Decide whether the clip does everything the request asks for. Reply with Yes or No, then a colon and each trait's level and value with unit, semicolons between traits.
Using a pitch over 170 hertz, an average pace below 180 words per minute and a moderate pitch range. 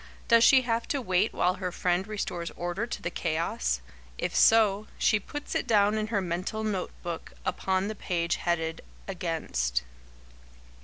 Yes: high, 190 Hz; average, 160 wpm; average, 4.0 semitones